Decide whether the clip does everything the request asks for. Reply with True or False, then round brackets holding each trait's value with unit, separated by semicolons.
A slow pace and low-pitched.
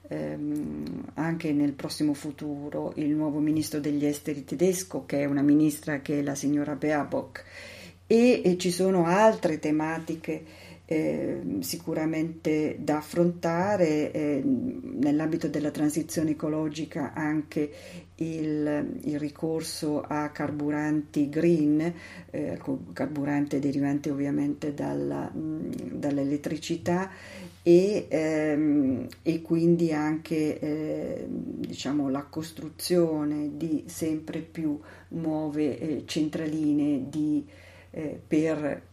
False (100 wpm; 150 Hz)